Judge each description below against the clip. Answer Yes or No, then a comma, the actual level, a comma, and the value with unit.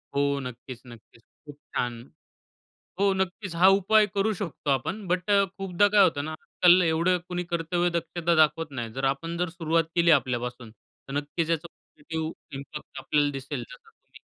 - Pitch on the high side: No, medium, 165 Hz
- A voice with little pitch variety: No, average, 4.2 semitones